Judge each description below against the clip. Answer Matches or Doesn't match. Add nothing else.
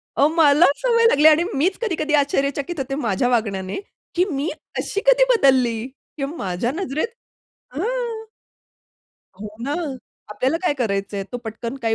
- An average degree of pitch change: Doesn't match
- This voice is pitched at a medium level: Doesn't match